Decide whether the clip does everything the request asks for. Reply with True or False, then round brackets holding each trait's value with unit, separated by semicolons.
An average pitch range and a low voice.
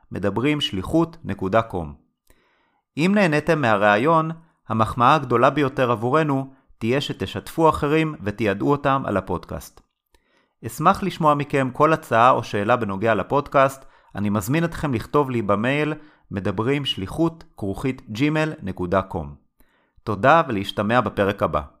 False (6.5 semitones; 130 Hz)